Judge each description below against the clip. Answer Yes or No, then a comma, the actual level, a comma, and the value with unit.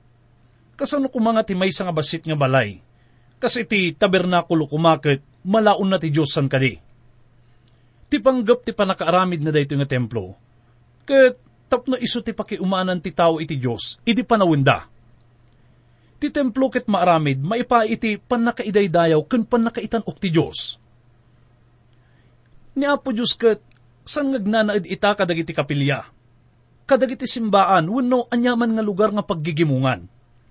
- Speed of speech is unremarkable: No, slow, 130 wpm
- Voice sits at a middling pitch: Yes, medium, 170 Hz